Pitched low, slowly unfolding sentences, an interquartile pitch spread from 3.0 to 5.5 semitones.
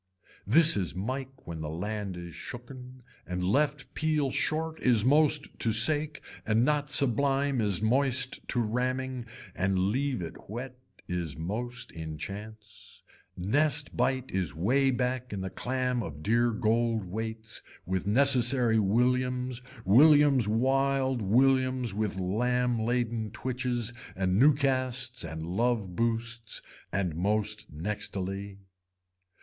Yes: low, 120 Hz; slow, 125 wpm; average, 4.6 semitones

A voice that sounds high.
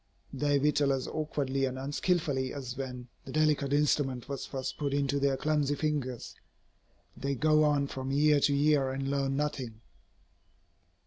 No: medium, 140 Hz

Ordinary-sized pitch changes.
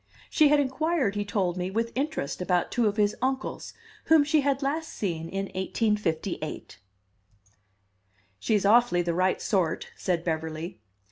No: wide, 7.0 semitones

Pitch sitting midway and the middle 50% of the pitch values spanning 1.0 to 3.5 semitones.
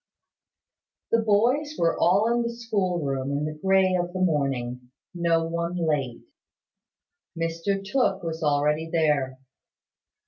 No: medium, 170 Hz; average, 4.6 semitones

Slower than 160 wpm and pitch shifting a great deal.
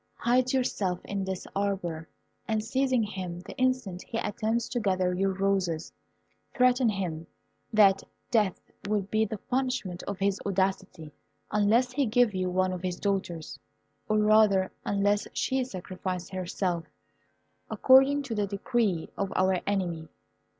No: average, 140 wpm; average, 3.5 semitones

